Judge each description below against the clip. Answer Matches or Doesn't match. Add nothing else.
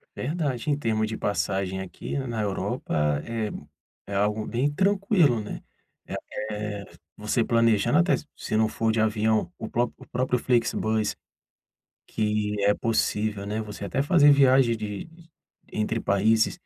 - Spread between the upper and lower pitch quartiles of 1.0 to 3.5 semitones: Matches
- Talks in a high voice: Doesn't match